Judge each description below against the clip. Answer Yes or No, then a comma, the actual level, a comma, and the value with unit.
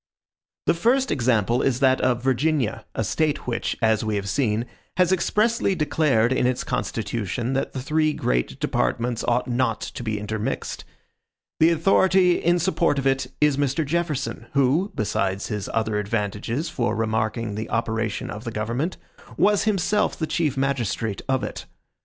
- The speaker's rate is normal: Yes, average, 160 wpm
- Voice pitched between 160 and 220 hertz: No, low, 130 Hz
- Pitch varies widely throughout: Yes, wide, 5.9 semitones